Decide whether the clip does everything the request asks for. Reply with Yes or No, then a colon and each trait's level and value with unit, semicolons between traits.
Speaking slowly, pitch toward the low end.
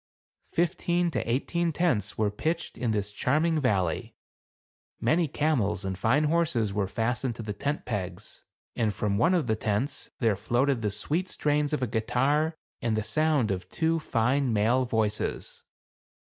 No: average, 160 wpm; low, 120 Hz